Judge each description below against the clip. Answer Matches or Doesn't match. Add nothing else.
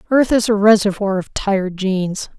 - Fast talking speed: Doesn't match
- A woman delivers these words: Matches